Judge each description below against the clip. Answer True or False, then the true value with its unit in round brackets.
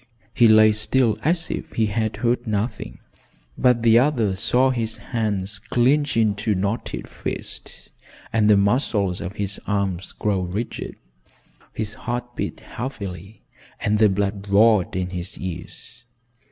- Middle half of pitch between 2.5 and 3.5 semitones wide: True (3.1 semitones)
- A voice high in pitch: False (105 Hz)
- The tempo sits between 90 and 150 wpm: True (140 wpm)